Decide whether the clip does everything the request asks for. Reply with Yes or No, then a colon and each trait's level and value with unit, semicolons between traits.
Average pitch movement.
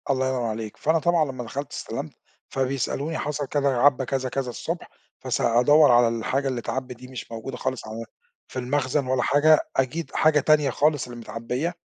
Yes: average, 3.0 semitones